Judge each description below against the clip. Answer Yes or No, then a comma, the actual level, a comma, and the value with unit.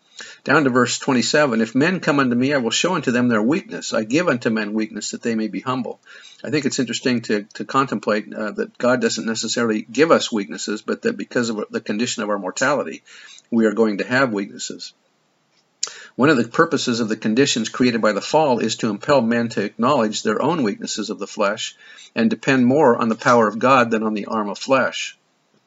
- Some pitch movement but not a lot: Yes, average, 3.4 semitones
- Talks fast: Yes, fast, 215 wpm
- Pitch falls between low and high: No, low, 120 Hz